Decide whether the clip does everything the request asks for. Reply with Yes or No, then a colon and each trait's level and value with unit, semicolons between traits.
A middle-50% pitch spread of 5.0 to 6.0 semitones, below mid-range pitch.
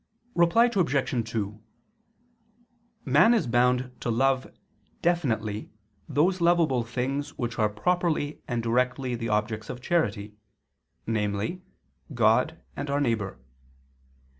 Yes: wide, 5.5 semitones; low, 125 Hz